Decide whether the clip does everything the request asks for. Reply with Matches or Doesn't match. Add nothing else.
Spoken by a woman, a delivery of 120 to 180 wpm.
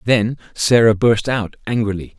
Doesn't match